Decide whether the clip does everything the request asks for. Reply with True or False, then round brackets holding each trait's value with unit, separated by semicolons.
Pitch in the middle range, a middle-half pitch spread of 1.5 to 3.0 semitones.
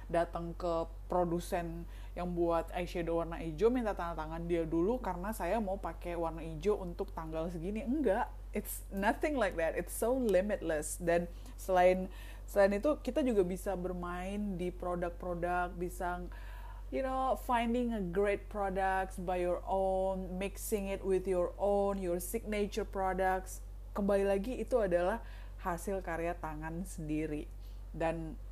True (180 Hz; 2.7 semitones)